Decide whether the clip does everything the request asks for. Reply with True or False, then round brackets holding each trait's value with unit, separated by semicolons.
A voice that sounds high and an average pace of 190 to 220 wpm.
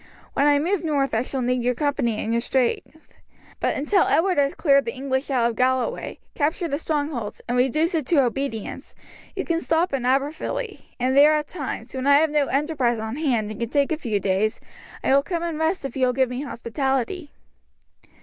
True (275 Hz; 205 wpm)